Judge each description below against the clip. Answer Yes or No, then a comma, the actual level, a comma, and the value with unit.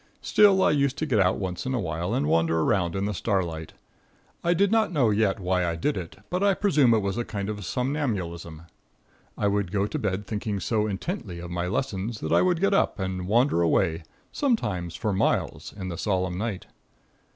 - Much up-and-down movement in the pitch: Yes, wide, 6.1 semitones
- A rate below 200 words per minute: No, fast, 205 wpm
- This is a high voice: No, low, 100 Hz